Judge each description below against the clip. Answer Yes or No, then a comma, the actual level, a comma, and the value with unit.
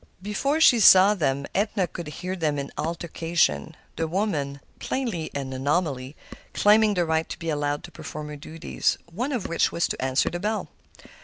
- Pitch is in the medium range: Yes, medium, 165 Hz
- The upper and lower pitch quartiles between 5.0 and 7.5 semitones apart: Yes, wide, 5.5 semitones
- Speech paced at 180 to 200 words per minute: No, average, 165 wpm